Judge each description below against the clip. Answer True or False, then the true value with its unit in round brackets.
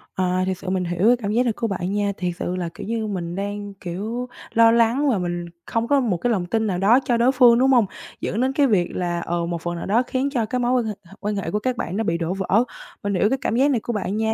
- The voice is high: True (210 Hz)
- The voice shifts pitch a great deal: False (4.6 semitones)